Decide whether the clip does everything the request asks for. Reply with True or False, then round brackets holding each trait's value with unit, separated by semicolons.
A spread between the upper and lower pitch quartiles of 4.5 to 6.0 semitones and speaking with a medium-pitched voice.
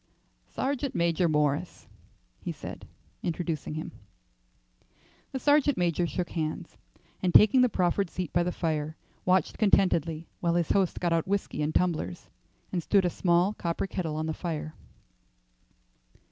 False (3.0 semitones; 175 Hz)